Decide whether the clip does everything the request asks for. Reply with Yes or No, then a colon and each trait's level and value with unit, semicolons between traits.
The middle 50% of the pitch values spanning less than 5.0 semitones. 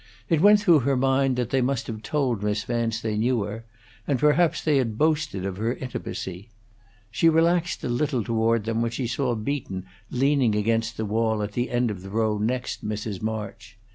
Yes: average, 3.9 semitones